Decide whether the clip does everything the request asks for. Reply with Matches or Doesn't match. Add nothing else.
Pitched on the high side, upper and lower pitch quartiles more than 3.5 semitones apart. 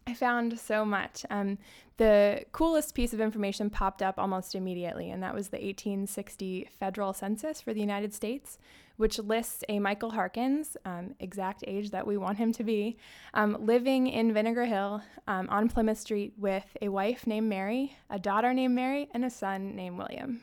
Doesn't match